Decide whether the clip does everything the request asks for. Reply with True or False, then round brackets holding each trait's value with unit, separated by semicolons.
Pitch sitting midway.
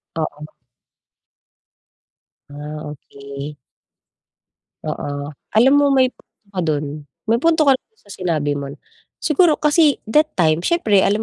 True (180 Hz)